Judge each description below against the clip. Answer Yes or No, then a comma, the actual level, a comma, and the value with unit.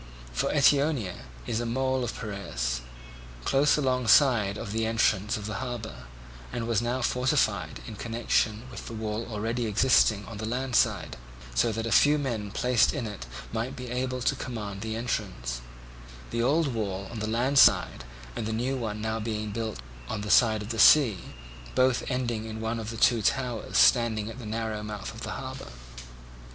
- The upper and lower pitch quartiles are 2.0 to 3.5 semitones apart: Yes, average, 2.9 semitones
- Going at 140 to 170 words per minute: No, average, 185 wpm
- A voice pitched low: Yes, low, 115 Hz